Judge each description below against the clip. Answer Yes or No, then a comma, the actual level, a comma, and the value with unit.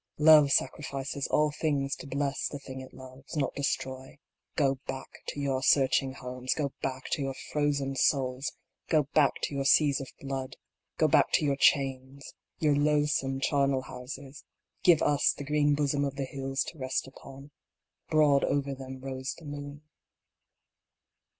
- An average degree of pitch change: No, narrow, 1.5 semitones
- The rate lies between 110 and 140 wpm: No, average, 160 wpm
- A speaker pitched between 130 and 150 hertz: Yes, medium, 140 Hz